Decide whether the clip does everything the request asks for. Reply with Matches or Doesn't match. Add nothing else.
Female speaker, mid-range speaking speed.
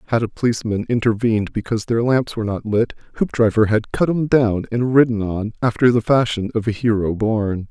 Doesn't match